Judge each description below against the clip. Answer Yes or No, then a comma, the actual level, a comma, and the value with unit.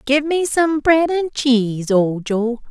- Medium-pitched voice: No, very high, 265 Hz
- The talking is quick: No, average, 155 wpm